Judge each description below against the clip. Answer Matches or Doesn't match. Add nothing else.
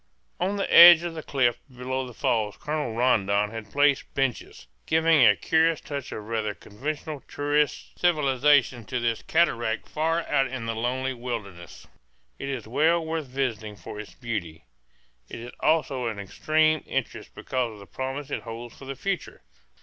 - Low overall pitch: Matches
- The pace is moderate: Matches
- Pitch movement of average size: Matches